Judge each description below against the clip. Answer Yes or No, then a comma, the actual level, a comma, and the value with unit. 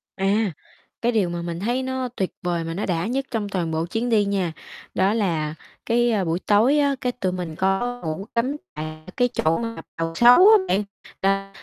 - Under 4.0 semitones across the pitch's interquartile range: No, wide, 5.6 semitones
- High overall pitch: Yes, high, 195 Hz